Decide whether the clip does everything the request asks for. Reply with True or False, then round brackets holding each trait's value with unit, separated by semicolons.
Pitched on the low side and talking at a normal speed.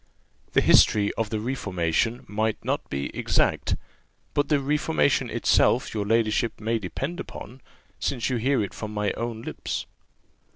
True (110 Hz; 150 wpm)